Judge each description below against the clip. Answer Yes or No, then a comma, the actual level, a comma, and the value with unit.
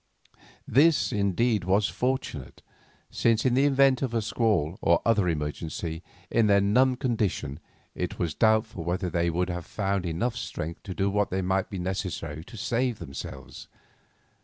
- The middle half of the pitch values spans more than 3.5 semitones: Yes, average, 5.2 semitones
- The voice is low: Yes, low, 100 Hz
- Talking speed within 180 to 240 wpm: No, average, 155 wpm